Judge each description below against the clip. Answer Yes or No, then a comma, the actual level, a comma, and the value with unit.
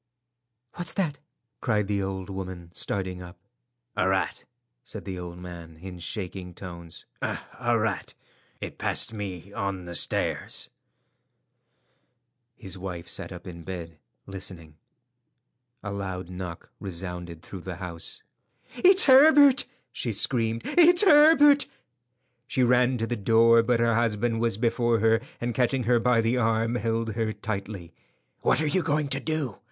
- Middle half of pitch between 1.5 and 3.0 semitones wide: No, average, 4.9 semitones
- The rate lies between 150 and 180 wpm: No, average, 140 wpm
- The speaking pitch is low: Yes, low, 105 Hz